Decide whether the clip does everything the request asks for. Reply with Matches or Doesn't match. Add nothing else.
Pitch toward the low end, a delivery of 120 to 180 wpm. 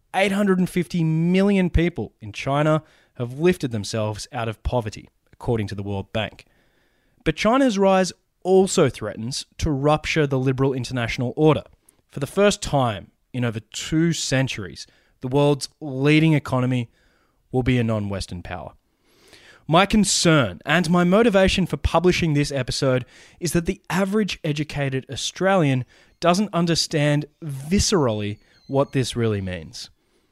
Doesn't match